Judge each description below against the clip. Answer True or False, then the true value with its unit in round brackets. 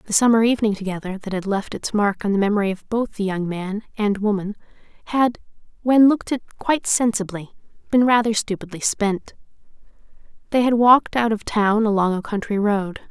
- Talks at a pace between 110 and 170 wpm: False (180 wpm)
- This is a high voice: True (210 Hz)